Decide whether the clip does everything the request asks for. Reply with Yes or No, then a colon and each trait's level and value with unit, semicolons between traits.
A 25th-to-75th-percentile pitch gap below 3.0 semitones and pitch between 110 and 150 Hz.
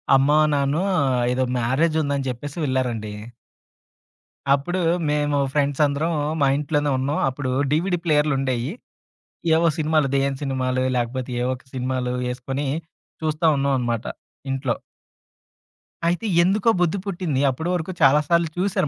No: average, 3.3 semitones; medium, 140 Hz